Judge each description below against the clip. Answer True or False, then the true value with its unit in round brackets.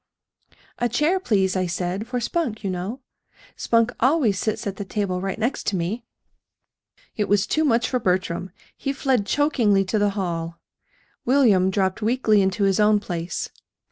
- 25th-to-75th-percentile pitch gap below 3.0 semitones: False (4.3 semitones)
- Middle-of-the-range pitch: False (205 Hz)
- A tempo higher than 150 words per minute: True (165 wpm)